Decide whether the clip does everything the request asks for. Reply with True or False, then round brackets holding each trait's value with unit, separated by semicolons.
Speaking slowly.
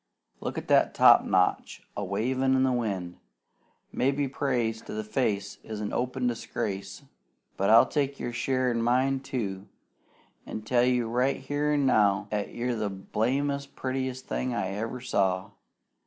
False (155 wpm)